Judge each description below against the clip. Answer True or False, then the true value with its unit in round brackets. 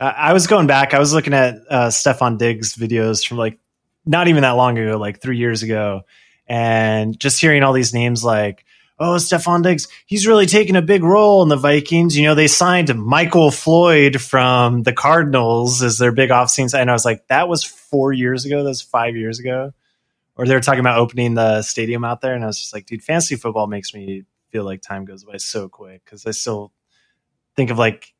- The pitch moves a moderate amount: True (4.7 semitones)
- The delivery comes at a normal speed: False (220 wpm)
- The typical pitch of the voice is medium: False (125 Hz)